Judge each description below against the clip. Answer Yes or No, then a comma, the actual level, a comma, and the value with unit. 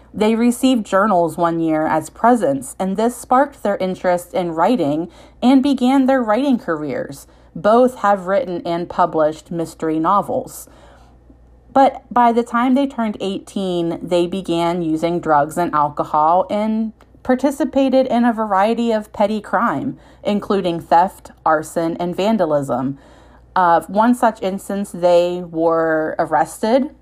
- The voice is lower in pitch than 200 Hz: Yes, high, 190 Hz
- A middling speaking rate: No, slow, 130 wpm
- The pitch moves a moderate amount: No, wide, 5.8 semitones